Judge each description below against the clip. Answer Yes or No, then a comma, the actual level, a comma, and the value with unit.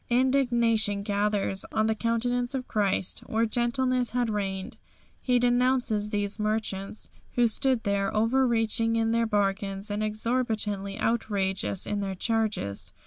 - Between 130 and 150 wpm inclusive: Yes, slow, 135 wpm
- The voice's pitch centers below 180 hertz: No, high, 220 Hz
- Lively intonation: No, average, 2.9 semitones